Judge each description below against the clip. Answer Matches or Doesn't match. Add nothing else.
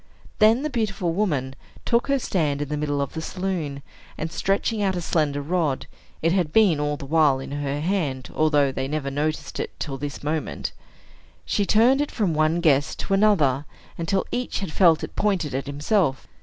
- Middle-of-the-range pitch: Matches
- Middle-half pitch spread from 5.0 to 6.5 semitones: Matches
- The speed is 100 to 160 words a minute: Doesn't match